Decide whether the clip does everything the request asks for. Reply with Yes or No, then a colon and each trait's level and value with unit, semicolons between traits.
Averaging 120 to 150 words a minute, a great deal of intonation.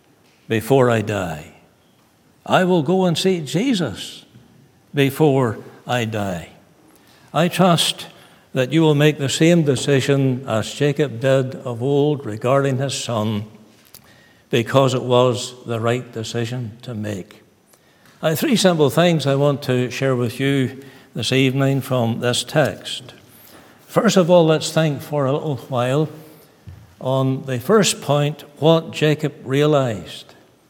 No: slow, 135 wpm; average, 4.1 semitones